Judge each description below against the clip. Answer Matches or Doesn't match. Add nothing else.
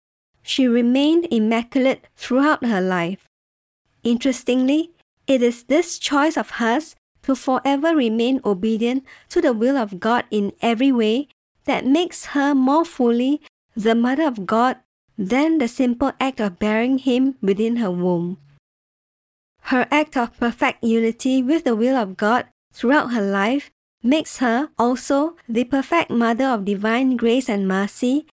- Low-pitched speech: Doesn't match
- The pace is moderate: Matches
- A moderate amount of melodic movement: Matches